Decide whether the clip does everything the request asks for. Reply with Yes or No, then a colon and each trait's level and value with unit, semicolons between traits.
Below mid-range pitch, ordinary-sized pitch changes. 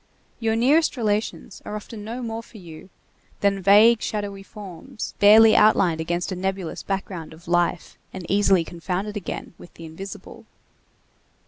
No: high, 200 Hz; average, 3.5 semitones